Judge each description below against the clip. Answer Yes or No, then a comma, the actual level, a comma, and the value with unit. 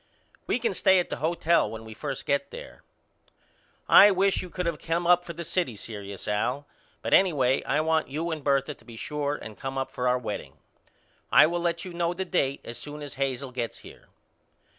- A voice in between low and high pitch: Yes, medium, 150 Hz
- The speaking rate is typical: No, fast, 210 wpm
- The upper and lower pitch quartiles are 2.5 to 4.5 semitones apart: No, average, 4.9 semitones